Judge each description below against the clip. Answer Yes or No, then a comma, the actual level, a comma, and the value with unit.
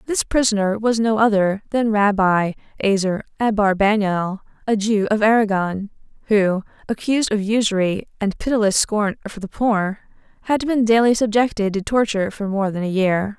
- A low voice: No, high, 210 Hz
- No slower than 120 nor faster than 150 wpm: Yes, average, 145 wpm